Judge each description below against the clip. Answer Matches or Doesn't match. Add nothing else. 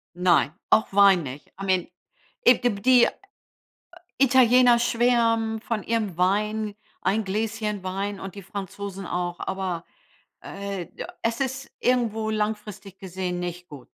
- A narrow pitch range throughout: Doesn't match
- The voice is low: Doesn't match